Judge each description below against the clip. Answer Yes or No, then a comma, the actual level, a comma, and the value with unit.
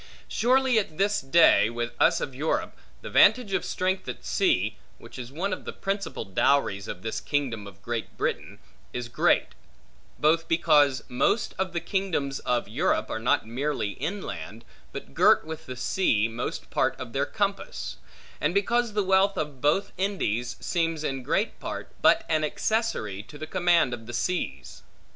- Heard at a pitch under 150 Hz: No, medium, 155 Hz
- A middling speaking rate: Yes, average, 170 wpm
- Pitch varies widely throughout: Yes, wide, 7.8 semitones